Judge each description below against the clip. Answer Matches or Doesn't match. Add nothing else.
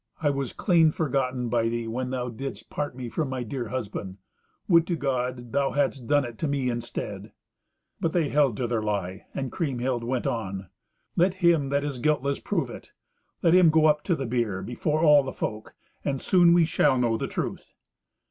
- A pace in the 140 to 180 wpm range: Doesn't match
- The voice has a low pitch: Matches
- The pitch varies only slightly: Doesn't match